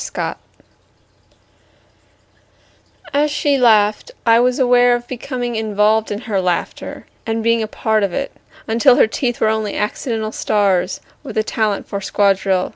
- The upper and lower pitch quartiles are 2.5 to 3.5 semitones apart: Yes, average, 2.8 semitones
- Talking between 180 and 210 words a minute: No, average, 145 wpm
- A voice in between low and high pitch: No, high, 220 Hz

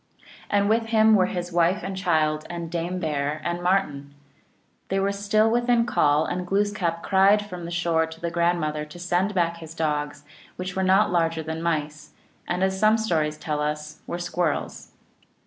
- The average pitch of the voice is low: No, medium, 175 Hz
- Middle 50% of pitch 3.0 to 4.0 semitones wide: Yes, average, 3.4 semitones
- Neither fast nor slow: Yes, average, 180 wpm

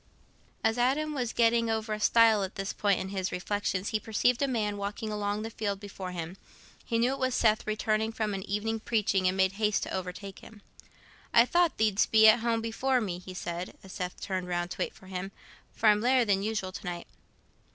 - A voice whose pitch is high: Yes, high, 210 Hz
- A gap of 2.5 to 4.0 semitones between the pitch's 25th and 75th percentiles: Yes, average, 2.9 semitones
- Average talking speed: No, fast, 215 wpm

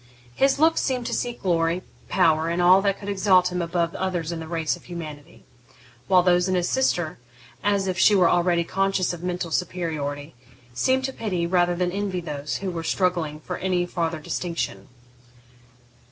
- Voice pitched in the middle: Yes, medium, 180 Hz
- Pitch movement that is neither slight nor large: No, narrow, 2.2 semitones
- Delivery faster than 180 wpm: No, average, 175 wpm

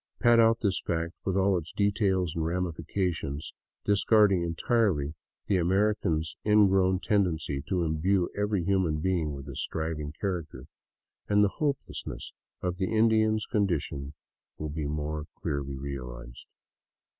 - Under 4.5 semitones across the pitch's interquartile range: No, average, 4.8 semitones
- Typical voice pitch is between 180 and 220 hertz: No, very low, 90 Hz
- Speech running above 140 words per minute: No, slow, 135 wpm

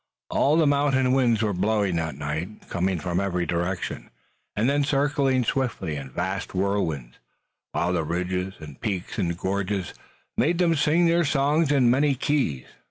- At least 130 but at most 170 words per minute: Yes, average, 160 wpm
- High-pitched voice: No, low, 100 Hz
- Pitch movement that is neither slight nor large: No, wide, 7.9 semitones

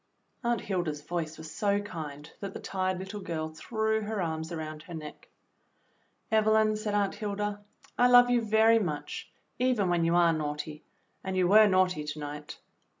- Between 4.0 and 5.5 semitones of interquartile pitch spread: Yes, average, 5.2 semitones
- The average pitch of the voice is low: No, medium, 185 Hz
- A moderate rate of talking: Yes, average, 170 wpm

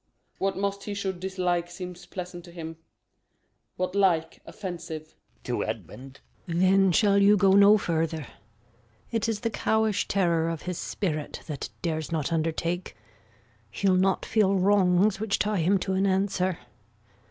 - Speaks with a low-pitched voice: No, medium, 185 Hz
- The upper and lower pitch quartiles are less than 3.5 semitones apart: Yes, average, 2.9 semitones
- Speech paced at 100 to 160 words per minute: Yes, average, 150 wpm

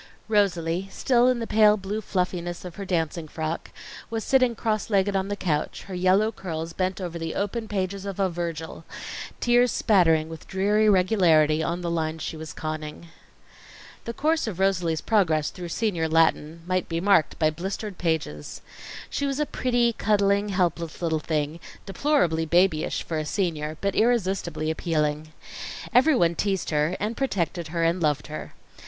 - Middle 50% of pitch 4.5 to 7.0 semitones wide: No, average, 4.1 semitones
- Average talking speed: Yes, average, 165 wpm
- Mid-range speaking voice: Yes, medium, 180 Hz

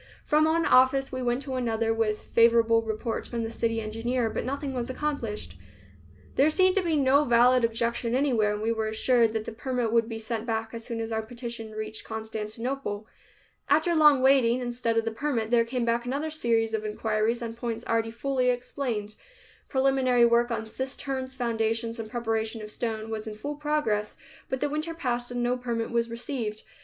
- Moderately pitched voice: No, high, 235 Hz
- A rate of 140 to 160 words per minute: No, average, 190 wpm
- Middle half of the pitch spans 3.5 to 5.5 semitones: No, narrow, 2.6 semitones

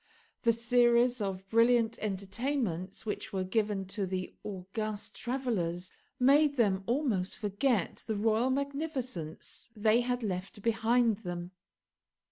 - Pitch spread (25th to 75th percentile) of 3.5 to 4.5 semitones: Yes, average, 4.1 semitones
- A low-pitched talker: No, high, 220 Hz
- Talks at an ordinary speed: No, slow, 115 wpm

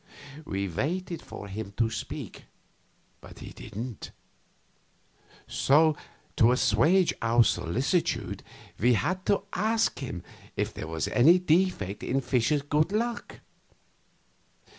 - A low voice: Yes, low, 130 Hz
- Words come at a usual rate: No, slow, 115 wpm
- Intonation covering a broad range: Yes, wide, 8.4 semitones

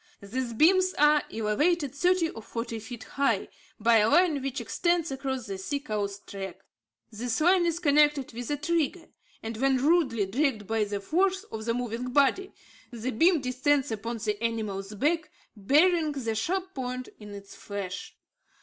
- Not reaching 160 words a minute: No, average, 165 wpm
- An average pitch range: No, wide, 5.7 semitones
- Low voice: No, very high, 255 Hz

